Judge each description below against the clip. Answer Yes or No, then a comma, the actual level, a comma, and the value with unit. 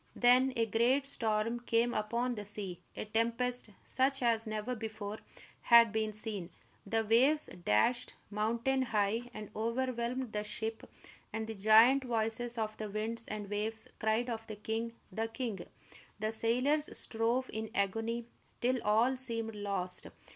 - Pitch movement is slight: Yes, narrow, 2.1 semitones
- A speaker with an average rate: Yes, average, 145 wpm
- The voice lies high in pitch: Yes, high, 225 Hz